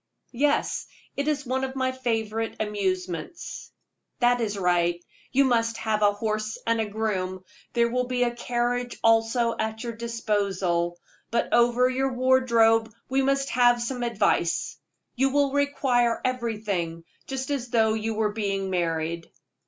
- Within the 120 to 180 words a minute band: Yes, average, 145 wpm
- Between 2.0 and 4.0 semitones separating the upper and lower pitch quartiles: Yes, average, 3.3 semitones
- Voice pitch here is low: No, high, 230 Hz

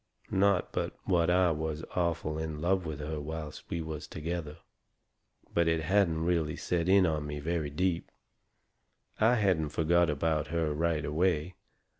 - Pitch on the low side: Yes, very low, 80 Hz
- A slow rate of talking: No, average, 155 wpm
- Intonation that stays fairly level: Yes, narrow, 2.3 semitones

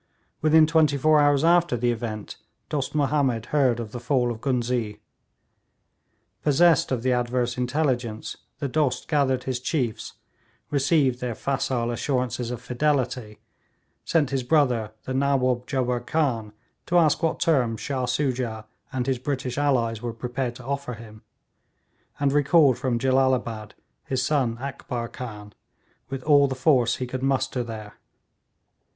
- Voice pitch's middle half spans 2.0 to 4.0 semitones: Yes, average, 2.8 semitones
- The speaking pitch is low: Yes, low, 130 Hz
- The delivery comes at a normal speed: Yes, average, 145 wpm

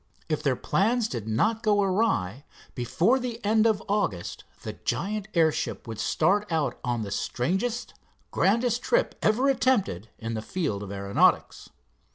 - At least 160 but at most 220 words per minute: No, average, 150 wpm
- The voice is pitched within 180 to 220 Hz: Yes, high, 190 Hz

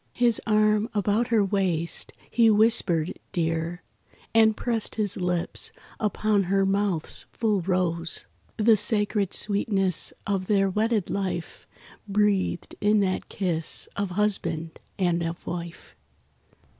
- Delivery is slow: Yes, slow, 120 wpm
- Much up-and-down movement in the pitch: No, average, 3.2 semitones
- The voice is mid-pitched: No, high, 200 Hz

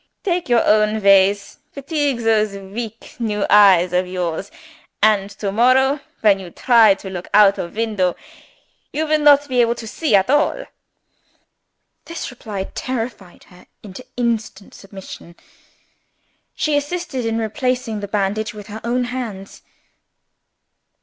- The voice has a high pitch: Yes, high, 220 Hz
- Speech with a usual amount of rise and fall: Yes, average, 4.3 semitones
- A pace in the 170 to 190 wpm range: No, slow, 135 wpm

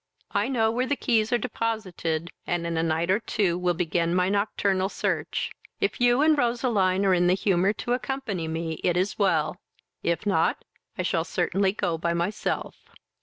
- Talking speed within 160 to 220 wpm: Yes, average, 180 wpm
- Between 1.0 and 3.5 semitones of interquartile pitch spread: No, average, 4.6 semitones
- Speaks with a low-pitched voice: No, high, 190 Hz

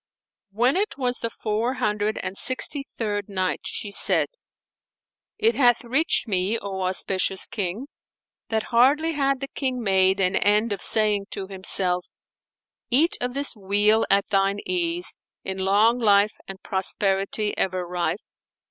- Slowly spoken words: No, average, 145 wpm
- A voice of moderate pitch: No, high, 210 Hz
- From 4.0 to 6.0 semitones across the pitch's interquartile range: Yes, average, 4.4 semitones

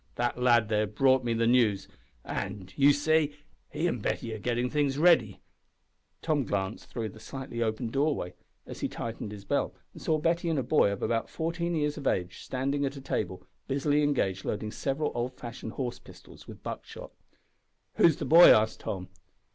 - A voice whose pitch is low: Yes, low, 125 Hz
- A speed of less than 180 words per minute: No, average, 185 wpm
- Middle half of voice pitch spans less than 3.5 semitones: No, average, 5.1 semitones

